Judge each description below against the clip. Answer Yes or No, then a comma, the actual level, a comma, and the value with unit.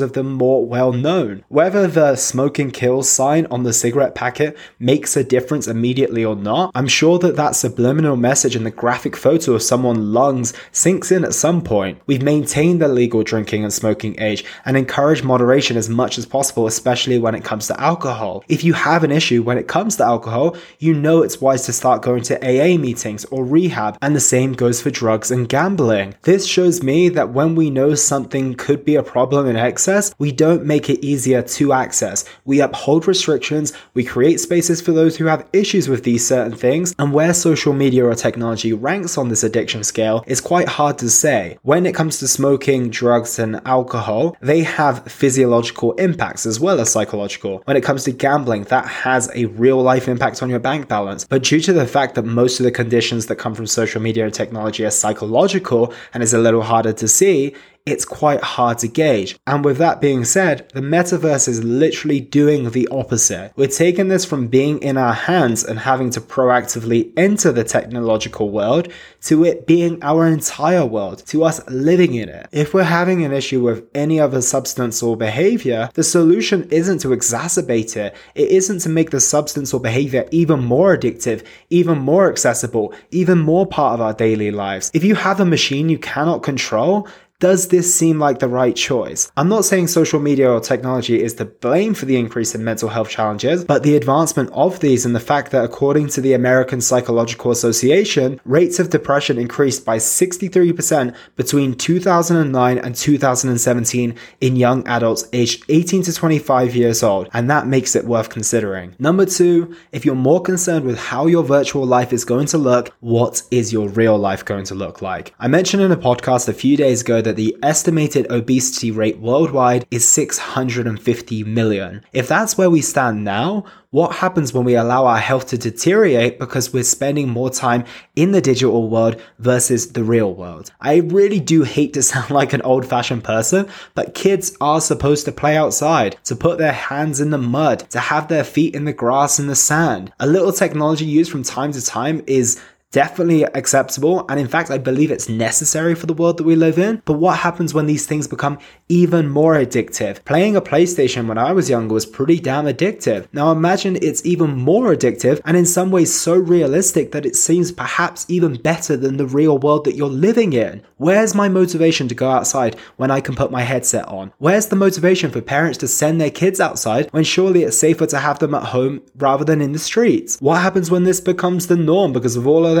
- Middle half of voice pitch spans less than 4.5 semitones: No, average, 5.2 semitones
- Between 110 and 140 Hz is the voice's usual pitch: Yes, low, 135 Hz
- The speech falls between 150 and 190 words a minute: No, average, 200 wpm